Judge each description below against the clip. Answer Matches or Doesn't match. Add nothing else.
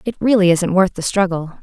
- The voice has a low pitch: Doesn't match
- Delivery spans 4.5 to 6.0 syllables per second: Matches